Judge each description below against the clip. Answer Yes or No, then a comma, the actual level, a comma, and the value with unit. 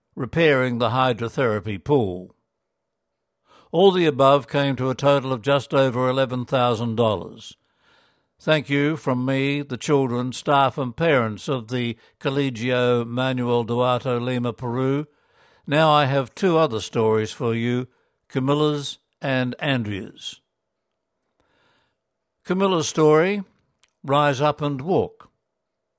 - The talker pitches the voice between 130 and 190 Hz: Yes, low, 135 Hz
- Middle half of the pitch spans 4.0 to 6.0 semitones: No, average, 2.9 semitones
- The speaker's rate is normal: No, slow, 110 wpm